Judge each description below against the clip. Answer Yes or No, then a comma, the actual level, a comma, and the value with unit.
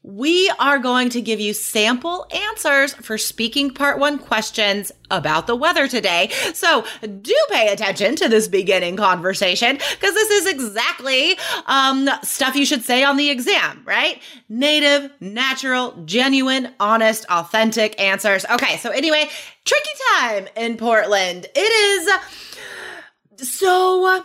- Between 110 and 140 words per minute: Yes, slow, 135 wpm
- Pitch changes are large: Yes, wide, 5.7 semitones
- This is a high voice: Yes, very high, 265 Hz